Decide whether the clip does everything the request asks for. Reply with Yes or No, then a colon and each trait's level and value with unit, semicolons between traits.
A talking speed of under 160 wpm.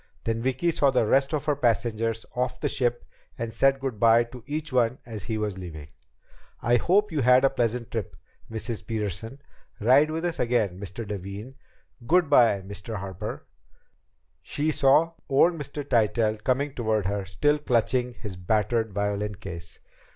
No: average, 165 wpm